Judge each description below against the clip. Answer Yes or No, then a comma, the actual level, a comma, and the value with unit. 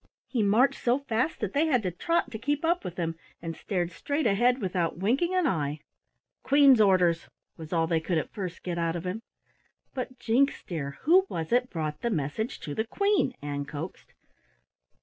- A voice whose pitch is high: Yes, high, 205 Hz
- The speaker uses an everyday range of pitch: No, wide, 7.9 semitones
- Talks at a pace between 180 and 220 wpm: Yes, average, 190 wpm